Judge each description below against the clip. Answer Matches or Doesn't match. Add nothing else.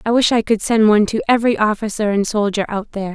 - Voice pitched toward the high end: Matches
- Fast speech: Matches